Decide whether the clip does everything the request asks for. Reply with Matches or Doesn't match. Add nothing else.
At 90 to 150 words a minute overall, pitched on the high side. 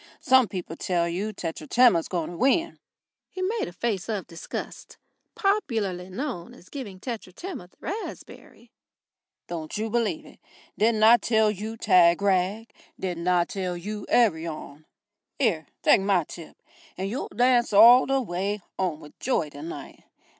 Matches